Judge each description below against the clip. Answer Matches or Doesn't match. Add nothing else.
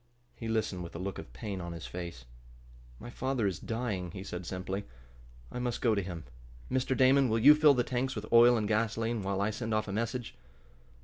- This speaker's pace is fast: Matches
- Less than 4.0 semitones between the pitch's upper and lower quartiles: Doesn't match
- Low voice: Matches